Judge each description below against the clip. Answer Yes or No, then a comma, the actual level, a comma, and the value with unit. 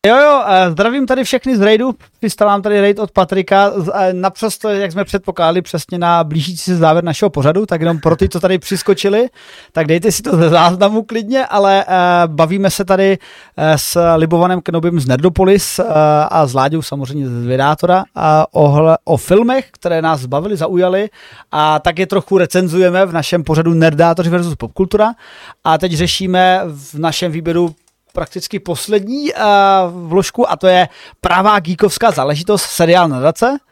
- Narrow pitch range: No, average, 3.5 semitones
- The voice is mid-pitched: Yes, medium, 180 Hz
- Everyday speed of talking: Yes, average, 155 wpm